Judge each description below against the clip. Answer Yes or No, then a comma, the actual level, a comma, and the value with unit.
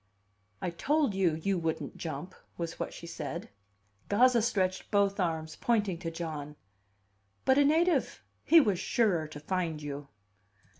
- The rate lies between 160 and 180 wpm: No, average, 145 wpm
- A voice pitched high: No, medium, 180 Hz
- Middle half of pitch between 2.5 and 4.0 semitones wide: No, average, 5.0 semitones